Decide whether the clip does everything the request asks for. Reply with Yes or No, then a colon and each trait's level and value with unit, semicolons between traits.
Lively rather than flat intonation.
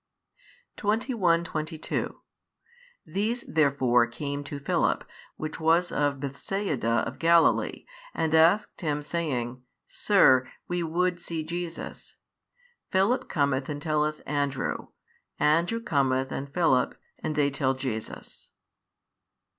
No: average, 3.6 semitones